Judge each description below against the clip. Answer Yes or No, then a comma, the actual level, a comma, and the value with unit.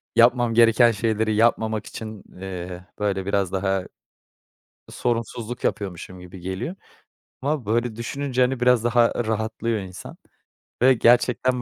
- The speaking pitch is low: Yes, low, 110 Hz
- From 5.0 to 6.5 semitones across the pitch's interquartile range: No, average, 3.7 semitones